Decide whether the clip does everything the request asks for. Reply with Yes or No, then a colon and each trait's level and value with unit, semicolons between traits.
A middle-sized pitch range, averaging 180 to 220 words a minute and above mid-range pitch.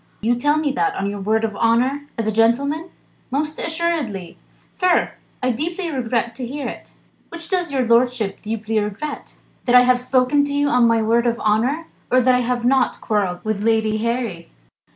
Yes: average, 4.3 semitones; average, 190 wpm; high, 245 Hz